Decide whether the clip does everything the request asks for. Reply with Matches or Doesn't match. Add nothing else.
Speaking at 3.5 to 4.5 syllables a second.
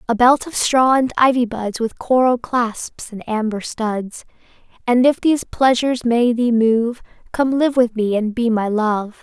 Matches